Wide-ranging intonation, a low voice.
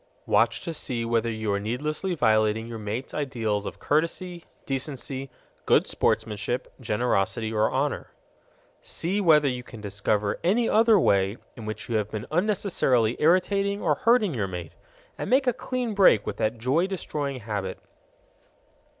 Yes: wide, 8.1 semitones; low, 125 Hz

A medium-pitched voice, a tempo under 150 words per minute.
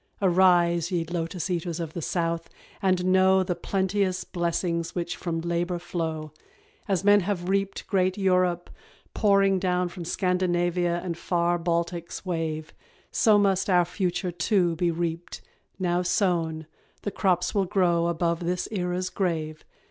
Yes: medium, 175 Hz; average, 140 wpm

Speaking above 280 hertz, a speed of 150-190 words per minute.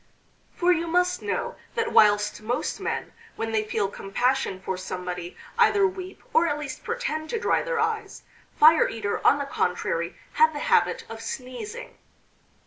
Yes: very high, 290 Hz; average, 160 wpm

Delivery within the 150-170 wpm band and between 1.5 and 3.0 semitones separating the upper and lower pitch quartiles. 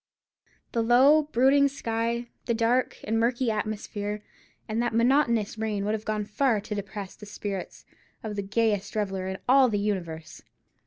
Yes: average, 160 wpm; narrow, 2.6 semitones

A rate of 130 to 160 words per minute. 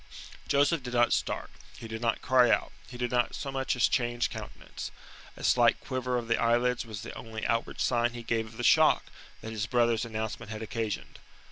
No: fast, 205 wpm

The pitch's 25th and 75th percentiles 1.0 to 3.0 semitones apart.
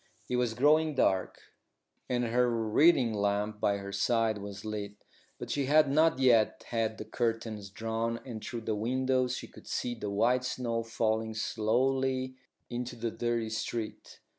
Yes: narrow, 2.5 semitones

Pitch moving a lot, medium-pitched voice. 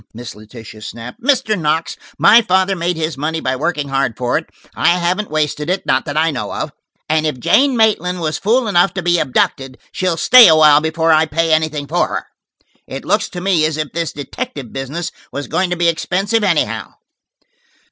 No: average, 3.7 semitones; medium, 160 Hz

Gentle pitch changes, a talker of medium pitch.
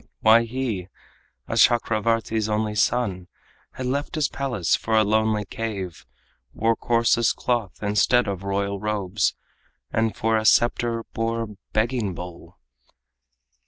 No: narrow, 2.3 semitones; low, 110 Hz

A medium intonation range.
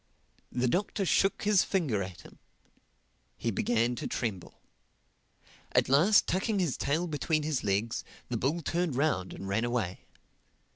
No: wide, 7.5 semitones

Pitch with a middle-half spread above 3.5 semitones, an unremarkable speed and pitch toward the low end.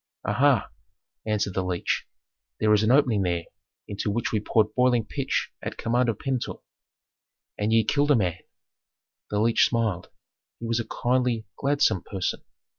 No: average, 3.0 semitones; average, 160 wpm; low, 110 Hz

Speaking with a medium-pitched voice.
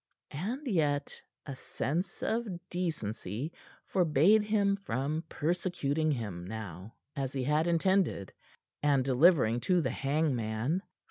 Yes: medium, 150 Hz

